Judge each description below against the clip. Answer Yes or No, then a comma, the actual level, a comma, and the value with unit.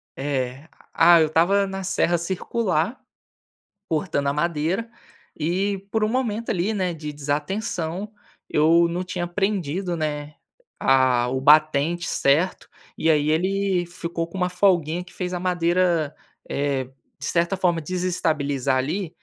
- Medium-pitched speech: Yes, medium, 170 Hz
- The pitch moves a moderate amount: Yes, average, 3.6 semitones